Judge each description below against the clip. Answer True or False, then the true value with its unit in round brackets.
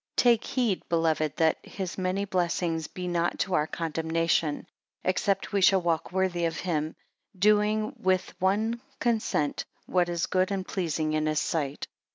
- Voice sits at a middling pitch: True (180 Hz)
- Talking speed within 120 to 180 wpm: True (155 wpm)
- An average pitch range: True (3.2 semitones)